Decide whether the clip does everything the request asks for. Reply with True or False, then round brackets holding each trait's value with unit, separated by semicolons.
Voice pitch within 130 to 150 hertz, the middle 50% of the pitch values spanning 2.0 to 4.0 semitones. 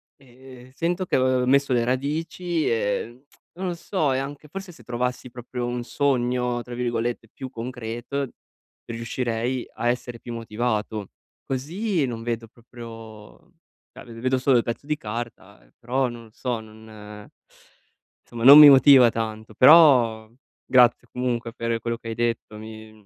False (120 Hz; 2.5 semitones)